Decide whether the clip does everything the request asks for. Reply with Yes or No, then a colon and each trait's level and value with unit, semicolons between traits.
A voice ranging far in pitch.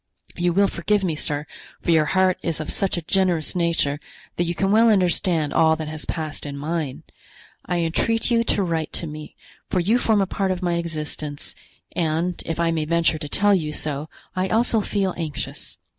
No: average, 3.4 semitones